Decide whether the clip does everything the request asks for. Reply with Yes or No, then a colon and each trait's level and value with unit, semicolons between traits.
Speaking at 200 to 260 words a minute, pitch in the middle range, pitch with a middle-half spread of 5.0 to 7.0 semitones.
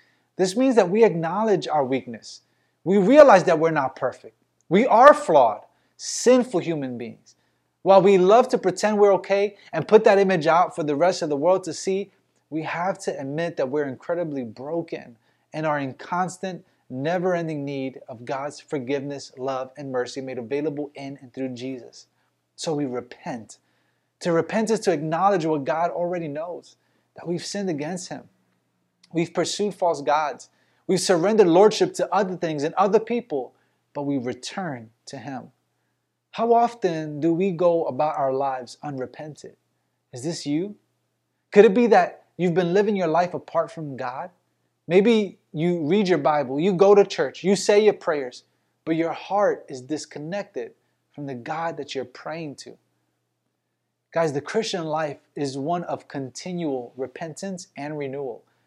No: average, 165 wpm; medium, 165 Hz; average, 5.3 semitones